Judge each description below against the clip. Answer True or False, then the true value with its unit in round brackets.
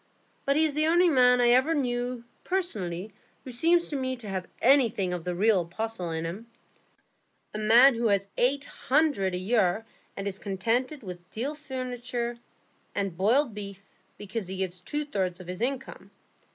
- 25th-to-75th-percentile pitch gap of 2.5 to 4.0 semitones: False (5.5 semitones)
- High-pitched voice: True (230 Hz)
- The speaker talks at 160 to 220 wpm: True (170 wpm)